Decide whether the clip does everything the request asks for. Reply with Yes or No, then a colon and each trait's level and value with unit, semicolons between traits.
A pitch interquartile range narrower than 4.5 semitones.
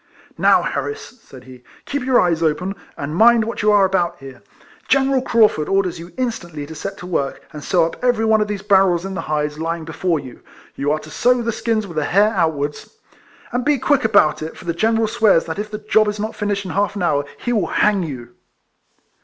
No: wide, 5.4 semitones